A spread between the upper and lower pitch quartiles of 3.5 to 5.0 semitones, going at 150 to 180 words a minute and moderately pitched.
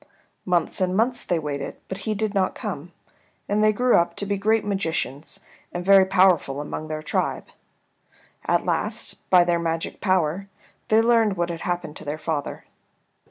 Yes: average, 3.9 semitones; average, 170 wpm; medium, 180 Hz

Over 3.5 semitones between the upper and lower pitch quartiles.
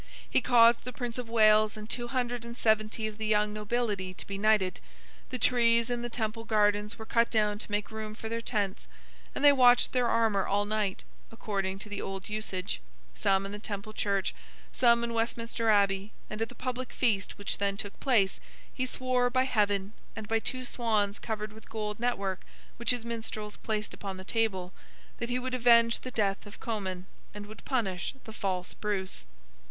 No: narrow, 2.6 semitones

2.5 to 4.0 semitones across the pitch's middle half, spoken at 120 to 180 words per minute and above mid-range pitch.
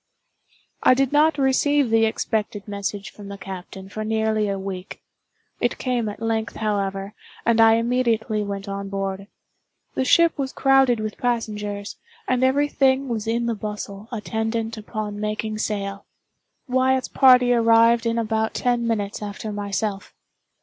Yes: average, 3.0 semitones; average, 150 wpm; high, 220 Hz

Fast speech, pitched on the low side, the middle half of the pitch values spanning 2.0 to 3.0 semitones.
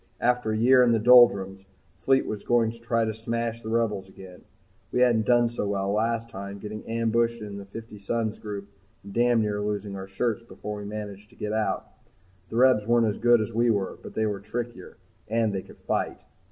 Yes: fast, 210 wpm; low, 110 Hz; narrow, 2.4 semitones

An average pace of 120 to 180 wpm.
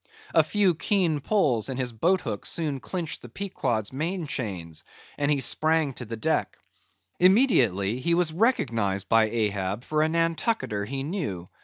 Yes: average, 160 wpm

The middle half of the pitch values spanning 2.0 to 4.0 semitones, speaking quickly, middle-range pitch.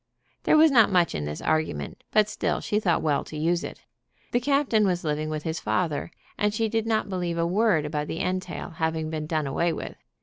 No: average, 5.2 semitones; fast, 215 wpm; medium, 170 Hz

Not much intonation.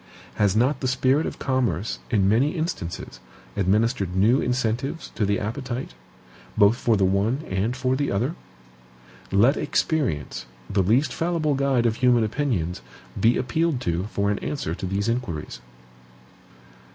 No: average, 5.2 semitones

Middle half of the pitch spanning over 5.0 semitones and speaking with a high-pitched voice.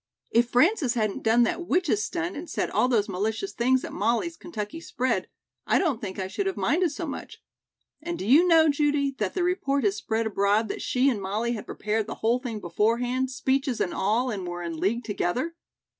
Yes: wide, 5.6 semitones; high, 240 Hz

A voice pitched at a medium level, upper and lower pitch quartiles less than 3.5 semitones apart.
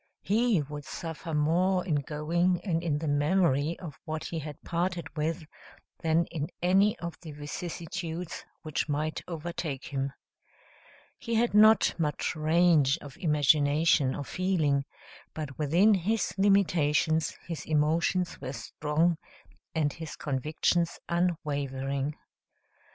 Yes: medium, 160 Hz; average, 3.0 semitones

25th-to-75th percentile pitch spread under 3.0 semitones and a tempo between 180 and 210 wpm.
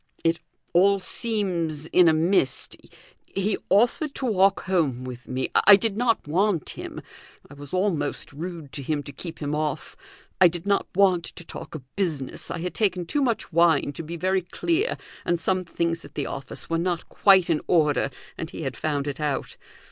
No: average, 4.4 semitones; average, 190 wpm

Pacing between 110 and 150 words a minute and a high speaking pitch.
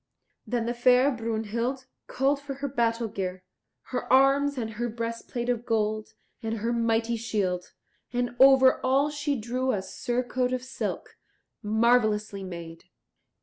Yes: average, 140 wpm; high, 235 Hz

